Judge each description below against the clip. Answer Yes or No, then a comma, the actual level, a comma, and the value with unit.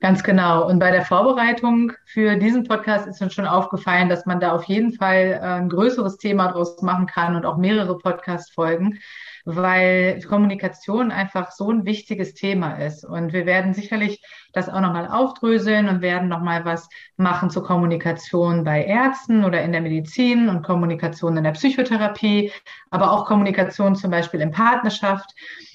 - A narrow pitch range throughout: No, average, 3.0 semitones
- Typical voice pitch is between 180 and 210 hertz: Yes, medium, 185 Hz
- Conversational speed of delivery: Yes, average, 165 wpm